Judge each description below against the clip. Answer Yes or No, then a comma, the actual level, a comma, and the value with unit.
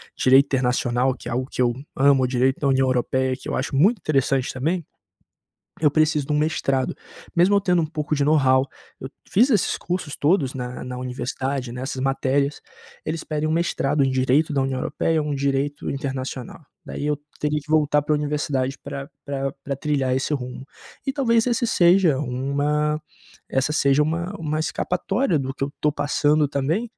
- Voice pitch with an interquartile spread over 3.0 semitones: No, average, 2.7 semitones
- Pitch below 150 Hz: Yes, medium, 140 Hz